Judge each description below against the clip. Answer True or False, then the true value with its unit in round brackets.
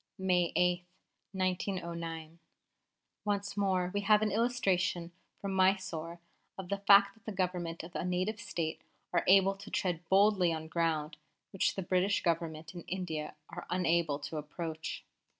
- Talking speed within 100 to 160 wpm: True (150 wpm)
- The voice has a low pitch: False (180 Hz)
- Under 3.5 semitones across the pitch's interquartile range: True (2.8 semitones)